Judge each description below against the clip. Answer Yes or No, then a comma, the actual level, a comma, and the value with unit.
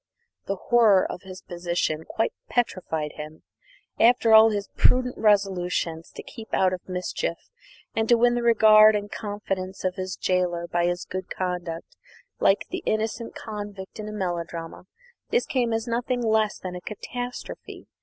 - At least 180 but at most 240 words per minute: No, average, 155 wpm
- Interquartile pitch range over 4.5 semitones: No, average, 3.8 semitones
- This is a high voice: Yes, high, 200 Hz